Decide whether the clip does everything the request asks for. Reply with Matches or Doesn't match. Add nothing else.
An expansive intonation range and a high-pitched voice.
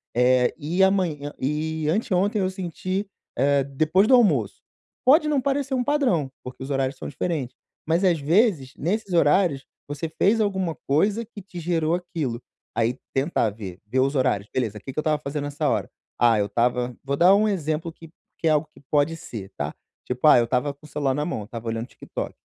Doesn't match